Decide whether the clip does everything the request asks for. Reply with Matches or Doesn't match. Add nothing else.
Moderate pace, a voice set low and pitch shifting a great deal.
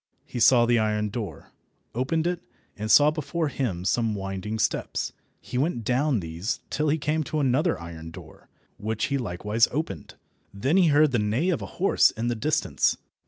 Matches